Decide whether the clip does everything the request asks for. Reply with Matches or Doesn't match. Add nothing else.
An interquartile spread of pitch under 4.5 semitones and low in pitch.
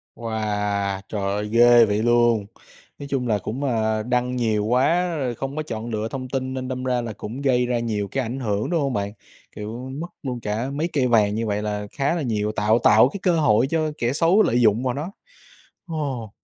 Matches